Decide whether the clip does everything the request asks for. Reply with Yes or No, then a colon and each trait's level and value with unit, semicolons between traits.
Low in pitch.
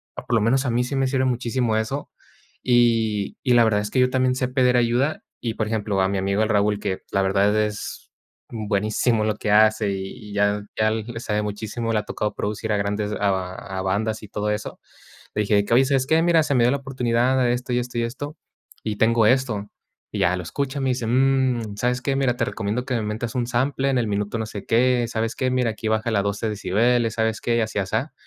Yes: low, 115 Hz